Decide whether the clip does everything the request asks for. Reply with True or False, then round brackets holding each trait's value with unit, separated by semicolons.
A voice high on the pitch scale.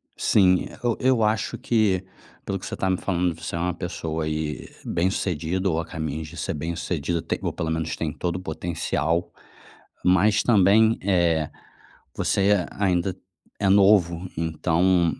False (90 Hz)